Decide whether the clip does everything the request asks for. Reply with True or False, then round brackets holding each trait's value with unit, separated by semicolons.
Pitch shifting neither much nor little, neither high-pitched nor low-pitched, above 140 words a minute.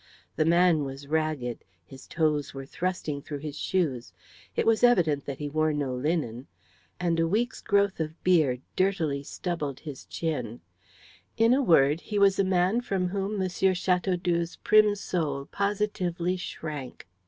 True (4.7 semitones; 165 Hz; 155 wpm)